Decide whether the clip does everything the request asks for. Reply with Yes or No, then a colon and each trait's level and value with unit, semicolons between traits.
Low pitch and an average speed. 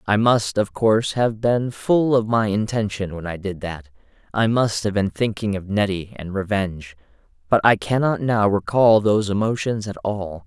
Yes: low, 105 Hz; average, 185 wpm